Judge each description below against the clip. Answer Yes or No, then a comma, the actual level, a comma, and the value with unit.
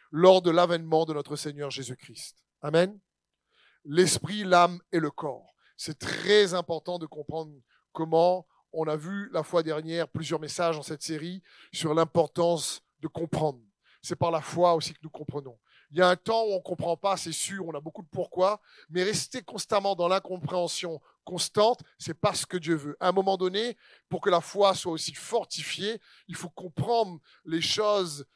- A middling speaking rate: Yes, average, 185 wpm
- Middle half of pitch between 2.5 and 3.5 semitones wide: Yes, average, 2.8 semitones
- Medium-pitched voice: Yes, medium, 170 Hz